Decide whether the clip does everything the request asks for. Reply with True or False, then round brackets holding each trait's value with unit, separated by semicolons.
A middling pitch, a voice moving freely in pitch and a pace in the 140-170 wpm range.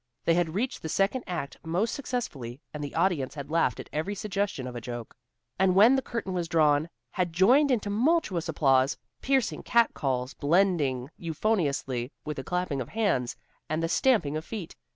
False (170 Hz; 6.3 semitones; 180 wpm)